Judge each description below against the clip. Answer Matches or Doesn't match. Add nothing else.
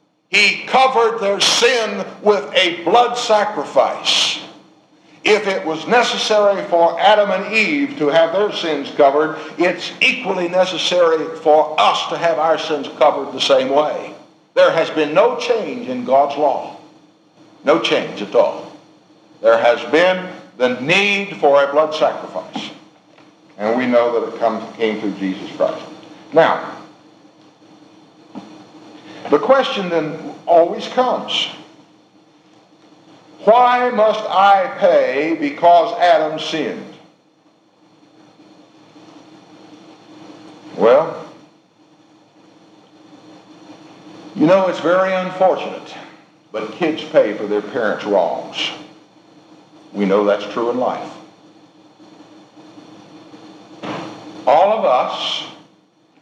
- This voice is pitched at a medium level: Matches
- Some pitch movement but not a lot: Doesn't match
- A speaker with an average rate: Doesn't match